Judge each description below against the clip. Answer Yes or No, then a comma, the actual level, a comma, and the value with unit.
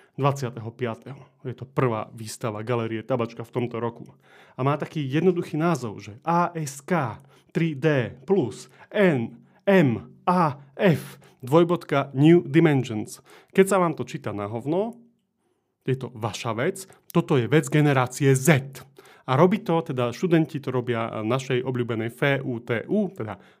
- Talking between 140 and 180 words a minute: No, average, 125 wpm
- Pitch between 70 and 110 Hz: No, low, 135 Hz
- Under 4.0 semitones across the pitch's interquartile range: No, wide, 5.5 semitones